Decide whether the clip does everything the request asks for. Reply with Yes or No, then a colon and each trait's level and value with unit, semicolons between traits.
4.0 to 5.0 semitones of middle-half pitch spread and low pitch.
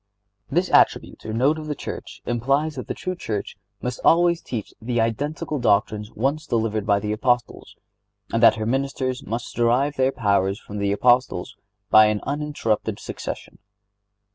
Yes: average, 4.3 semitones; low, 120 Hz